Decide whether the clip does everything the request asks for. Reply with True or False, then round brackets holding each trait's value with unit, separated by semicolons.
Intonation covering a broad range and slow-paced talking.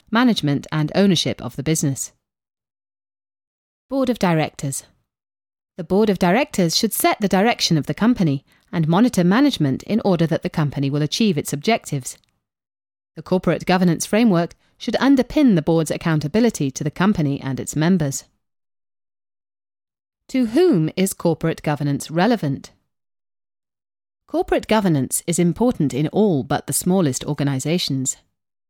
True (6.3 semitones; 130 wpm)